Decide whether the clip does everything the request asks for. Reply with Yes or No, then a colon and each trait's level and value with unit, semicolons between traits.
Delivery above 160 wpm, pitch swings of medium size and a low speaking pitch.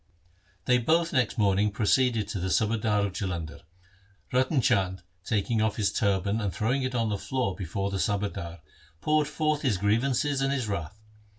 Yes: average, 170 wpm; average, 4.5 semitones; low, 105 Hz